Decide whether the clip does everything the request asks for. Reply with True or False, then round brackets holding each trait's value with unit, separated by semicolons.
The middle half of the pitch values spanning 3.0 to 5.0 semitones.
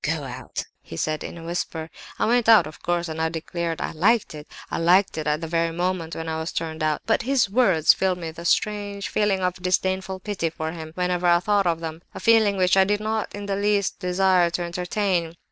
True (3.5 semitones)